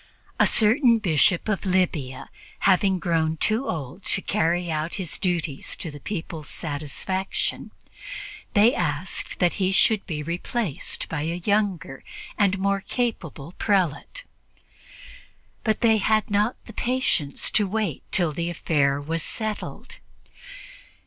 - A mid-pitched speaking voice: Yes, medium, 180 Hz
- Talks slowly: Yes, slow, 130 wpm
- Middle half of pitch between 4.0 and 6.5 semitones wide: Yes, average, 4.8 semitones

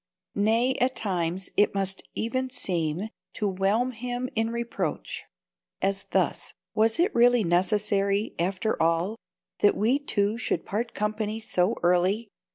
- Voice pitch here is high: Yes, high, 210 Hz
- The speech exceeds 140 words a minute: No, slow, 135 wpm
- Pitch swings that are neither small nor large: Yes, average, 3.4 semitones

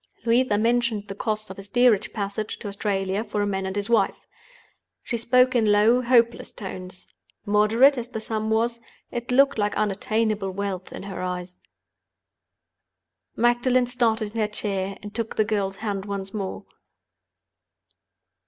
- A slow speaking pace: No, average, 155 wpm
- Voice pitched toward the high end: Yes, high, 215 Hz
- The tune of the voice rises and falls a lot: No, average, 2.9 semitones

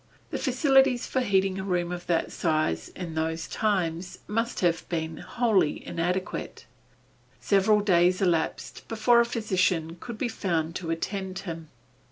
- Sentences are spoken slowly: No, average, 145 wpm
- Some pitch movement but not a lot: Yes, average, 4.4 semitones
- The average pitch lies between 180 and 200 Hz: Yes, medium, 185 Hz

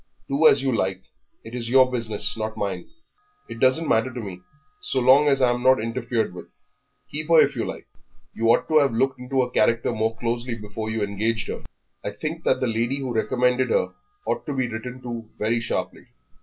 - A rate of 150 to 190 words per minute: No, fast, 205 wpm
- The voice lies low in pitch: Yes, low, 120 Hz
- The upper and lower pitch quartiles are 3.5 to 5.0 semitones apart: No, average, 2.7 semitones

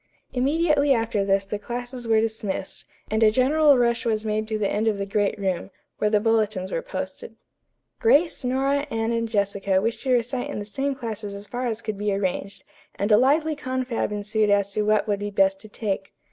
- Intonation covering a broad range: No, average, 3.7 semitones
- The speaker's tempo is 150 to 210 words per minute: Yes, fast, 205 wpm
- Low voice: No, high, 220 Hz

